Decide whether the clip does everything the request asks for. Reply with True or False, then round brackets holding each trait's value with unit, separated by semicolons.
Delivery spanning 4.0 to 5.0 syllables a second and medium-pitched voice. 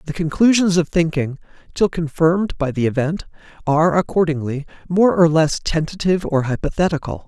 False (5.5 syllables/s; 160 Hz)